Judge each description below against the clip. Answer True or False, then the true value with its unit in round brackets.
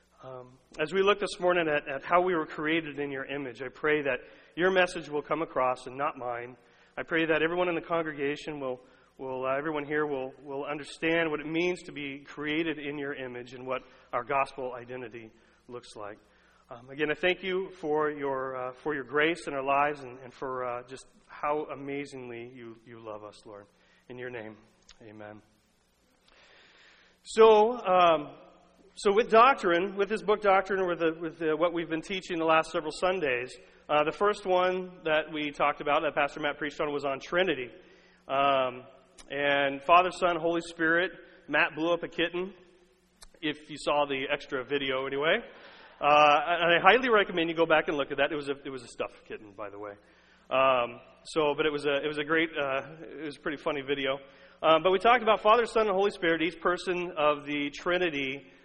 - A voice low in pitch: False (150 Hz)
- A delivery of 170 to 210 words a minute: True (200 wpm)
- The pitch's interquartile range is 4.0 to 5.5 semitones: True (4.4 semitones)